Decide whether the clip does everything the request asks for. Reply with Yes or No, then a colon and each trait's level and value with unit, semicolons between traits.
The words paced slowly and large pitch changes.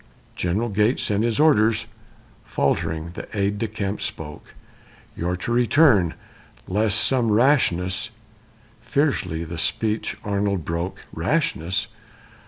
No: slow, 115 wpm; average, 4.3 semitones